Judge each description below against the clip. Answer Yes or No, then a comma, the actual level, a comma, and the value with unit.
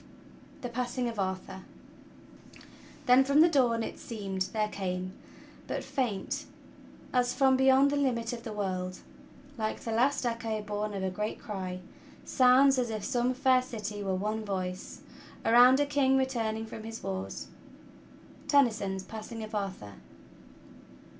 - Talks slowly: No, average, 150 wpm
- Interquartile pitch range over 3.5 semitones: Yes, average, 4.3 semitones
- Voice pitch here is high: Yes, high, 225 Hz